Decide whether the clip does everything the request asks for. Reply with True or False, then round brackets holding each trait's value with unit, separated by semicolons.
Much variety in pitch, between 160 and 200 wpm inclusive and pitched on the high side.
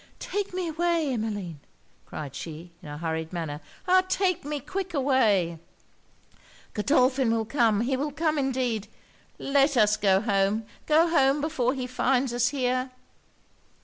False (6.0 semitones; 145 wpm; 255 Hz)